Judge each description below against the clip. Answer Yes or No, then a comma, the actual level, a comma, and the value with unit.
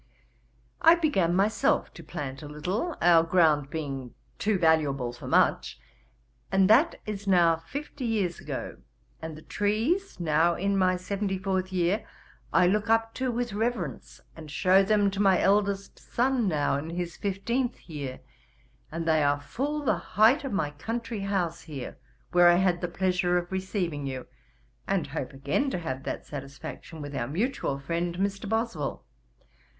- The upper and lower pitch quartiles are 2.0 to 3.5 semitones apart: No, average, 5.1 semitones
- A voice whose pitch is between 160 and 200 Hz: Yes, medium, 185 Hz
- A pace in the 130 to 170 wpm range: Yes, average, 160 wpm